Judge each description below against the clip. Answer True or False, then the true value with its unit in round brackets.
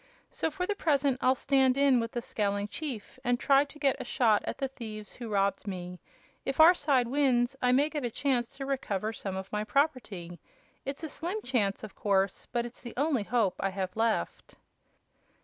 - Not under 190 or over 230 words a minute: True (200 wpm)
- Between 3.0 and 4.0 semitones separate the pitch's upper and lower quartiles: False (5.0 semitones)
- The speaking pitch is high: True (245 Hz)